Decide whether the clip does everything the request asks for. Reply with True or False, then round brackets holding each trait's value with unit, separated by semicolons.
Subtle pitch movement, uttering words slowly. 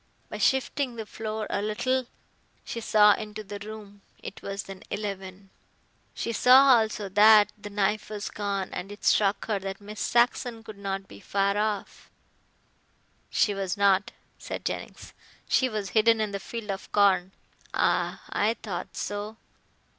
False (1.7 semitones; 155 wpm)